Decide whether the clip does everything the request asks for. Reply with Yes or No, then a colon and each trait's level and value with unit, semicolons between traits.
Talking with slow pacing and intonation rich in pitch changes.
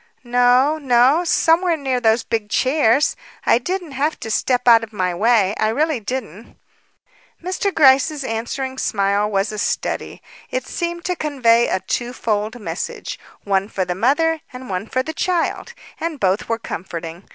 No: average, 165 wpm; wide, 5.7 semitones